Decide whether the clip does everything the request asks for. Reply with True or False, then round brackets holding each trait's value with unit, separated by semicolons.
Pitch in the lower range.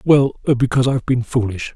True (125 Hz)